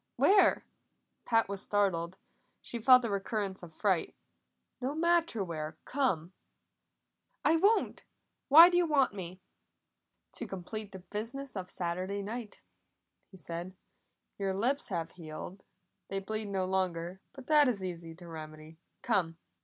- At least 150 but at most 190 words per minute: No, average, 140 wpm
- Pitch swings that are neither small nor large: No, wide, 5.7 semitones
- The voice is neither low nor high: No, high, 195 Hz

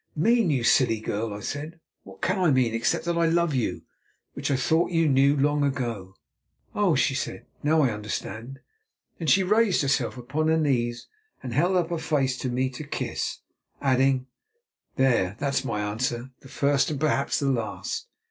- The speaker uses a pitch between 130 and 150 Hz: Yes, low, 135 Hz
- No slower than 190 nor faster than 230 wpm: No, average, 180 wpm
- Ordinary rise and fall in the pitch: Yes, average, 4.4 semitones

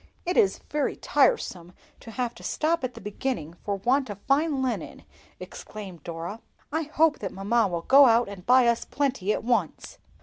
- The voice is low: No, high, 235 Hz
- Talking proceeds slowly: No, average, 180 wpm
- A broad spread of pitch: Yes, wide, 5.8 semitones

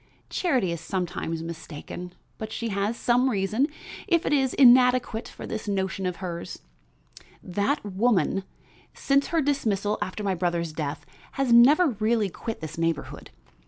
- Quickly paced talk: No, average, 145 wpm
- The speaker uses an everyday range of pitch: No, wide, 5.8 semitones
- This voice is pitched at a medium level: No, high, 205 Hz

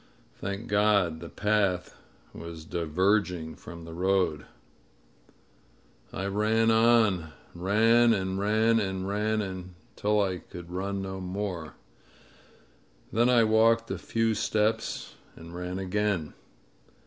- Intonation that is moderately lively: Yes, average, 3.2 semitones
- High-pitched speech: No, low, 100 Hz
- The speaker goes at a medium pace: No, slow, 115 wpm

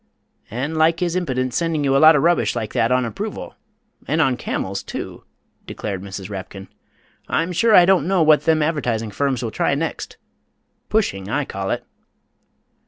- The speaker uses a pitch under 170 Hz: Yes, medium, 140 Hz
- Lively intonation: Yes, wide, 6.7 semitones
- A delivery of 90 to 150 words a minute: No, average, 170 wpm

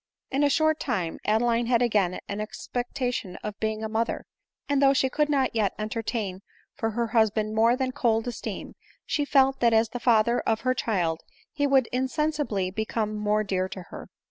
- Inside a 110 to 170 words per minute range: No, average, 185 wpm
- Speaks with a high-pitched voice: Yes, high, 230 Hz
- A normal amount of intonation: Yes, average, 3.4 semitones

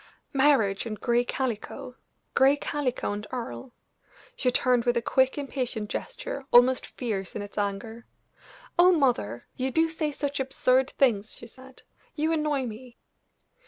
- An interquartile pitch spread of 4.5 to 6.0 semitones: No, average, 3.3 semitones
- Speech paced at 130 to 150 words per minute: Yes, average, 145 wpm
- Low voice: No, very high, 255 Hz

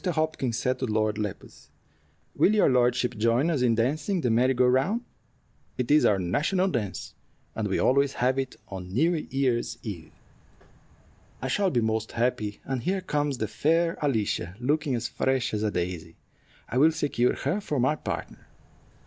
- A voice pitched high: No, low, 125 Hz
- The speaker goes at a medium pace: Yes, average, 170 wpm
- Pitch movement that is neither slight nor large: Yes, average, 4.9 semitones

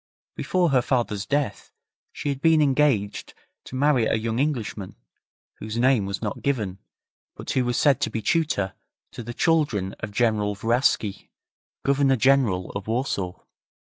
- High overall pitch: No, low, 120 Hz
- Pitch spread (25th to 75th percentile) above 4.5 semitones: Yes, average, 5.1 semitones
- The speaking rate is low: No, average, 150 wpm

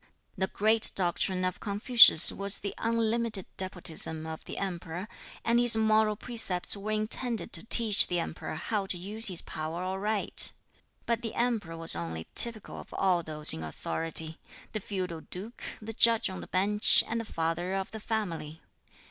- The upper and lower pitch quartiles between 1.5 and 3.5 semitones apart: No, average, 4.4 semitones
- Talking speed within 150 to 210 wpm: Yes, average, 165 wpm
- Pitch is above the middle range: Yes, high, 195 Hz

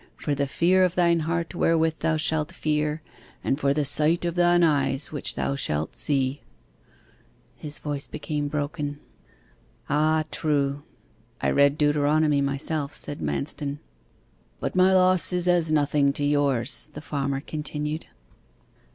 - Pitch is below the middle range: No, medium, 150 Hz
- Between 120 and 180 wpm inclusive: Yes, average, 140 wpm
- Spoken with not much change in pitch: Yes, narrow, 2.0 semitones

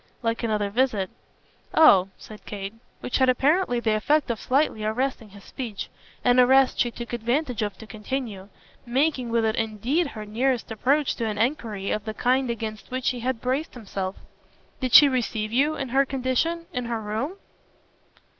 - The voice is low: No, high, 240 Hz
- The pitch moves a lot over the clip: No, average, 3.6 semitones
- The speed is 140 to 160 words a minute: No, average, 175 wpm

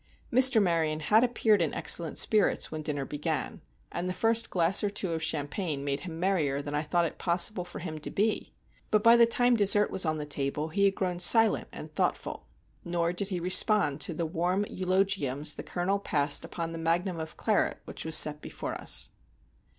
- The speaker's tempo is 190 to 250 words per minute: Yes, fast, 205 wpm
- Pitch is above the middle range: No, medium, 175 Hz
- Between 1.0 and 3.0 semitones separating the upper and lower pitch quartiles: No, average, 4.2 semitones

